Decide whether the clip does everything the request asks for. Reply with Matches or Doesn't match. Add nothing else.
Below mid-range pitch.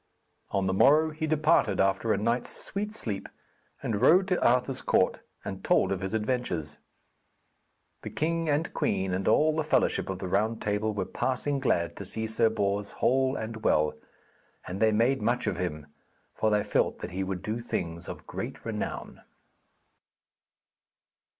Matches